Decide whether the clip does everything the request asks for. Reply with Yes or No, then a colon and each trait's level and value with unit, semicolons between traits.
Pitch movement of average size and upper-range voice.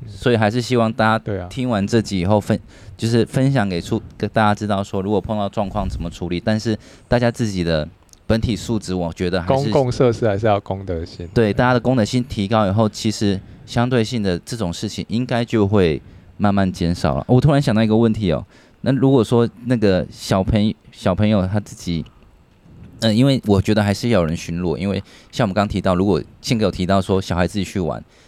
No: average, 3.5 semitones; low, 105 Hz